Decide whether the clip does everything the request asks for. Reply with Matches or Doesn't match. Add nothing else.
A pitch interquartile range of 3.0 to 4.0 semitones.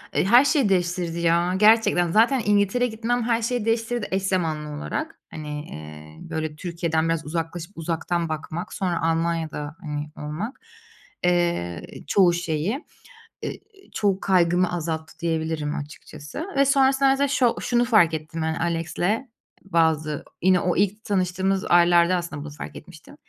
Doesn't match